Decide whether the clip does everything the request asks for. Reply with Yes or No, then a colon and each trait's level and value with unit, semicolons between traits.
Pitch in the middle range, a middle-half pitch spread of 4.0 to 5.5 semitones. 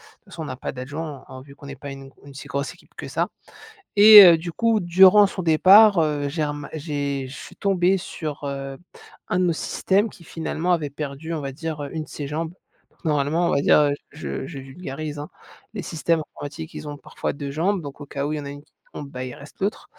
No: medium, 150 Hz; average, 3.5 semitones